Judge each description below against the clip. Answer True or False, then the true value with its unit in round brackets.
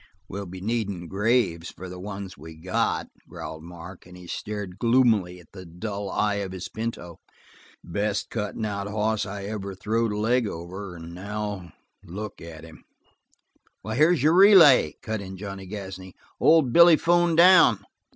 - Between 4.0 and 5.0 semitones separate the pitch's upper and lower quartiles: False (3.6 semitones)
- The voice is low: True (100 Hz)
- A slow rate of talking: False (160 wpm)